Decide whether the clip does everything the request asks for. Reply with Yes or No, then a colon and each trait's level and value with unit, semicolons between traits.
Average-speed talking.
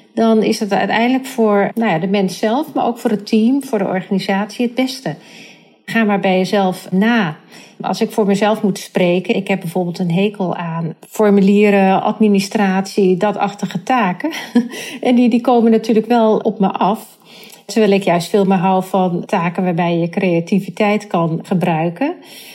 Yes: average, 170 wpm